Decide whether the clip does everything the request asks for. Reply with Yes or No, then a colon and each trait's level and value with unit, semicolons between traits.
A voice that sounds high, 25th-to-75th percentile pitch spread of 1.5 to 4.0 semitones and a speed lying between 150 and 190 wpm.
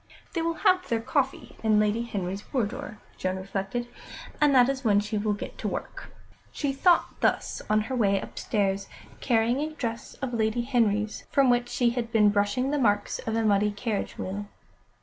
Yes: high, 225 Hz; average, 3.7 semitones; average, 185 wpm